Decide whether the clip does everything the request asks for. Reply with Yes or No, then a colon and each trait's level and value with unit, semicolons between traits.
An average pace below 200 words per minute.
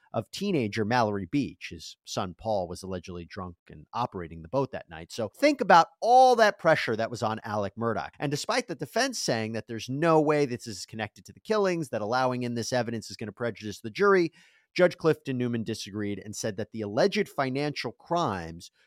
No: fast, 205 wpm